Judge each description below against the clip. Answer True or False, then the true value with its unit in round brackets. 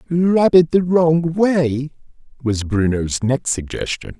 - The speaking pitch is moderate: True (145 Hz)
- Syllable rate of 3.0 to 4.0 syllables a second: True (3.5 syllables/s)